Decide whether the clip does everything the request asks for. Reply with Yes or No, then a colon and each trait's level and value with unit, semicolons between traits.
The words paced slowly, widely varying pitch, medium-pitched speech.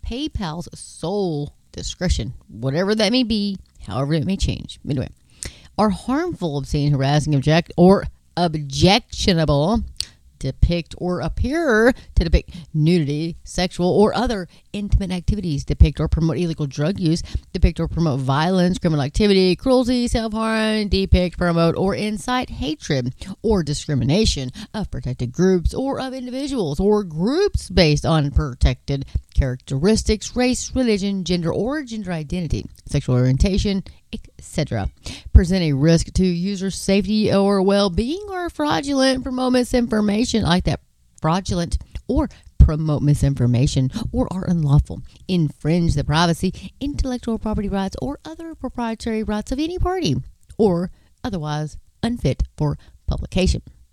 Yes: slow, 125 wpm; wide, 6.5 semitones; medium, 180 Hz